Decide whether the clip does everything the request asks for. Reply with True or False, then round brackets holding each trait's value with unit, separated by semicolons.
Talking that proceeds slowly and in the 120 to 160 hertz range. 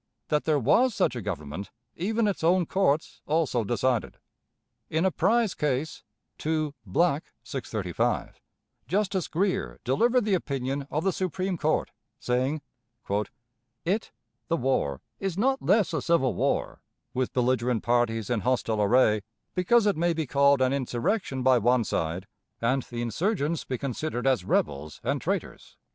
False (145 wpm; 140 Hz)